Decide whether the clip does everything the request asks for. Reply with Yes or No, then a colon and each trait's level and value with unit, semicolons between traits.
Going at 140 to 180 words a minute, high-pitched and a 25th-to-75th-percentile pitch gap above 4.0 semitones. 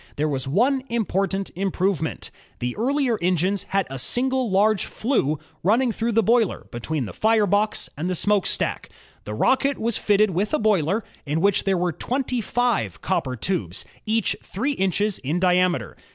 Yes: average, 165 wpm; high, 195 Hz; average, 4.6 semitones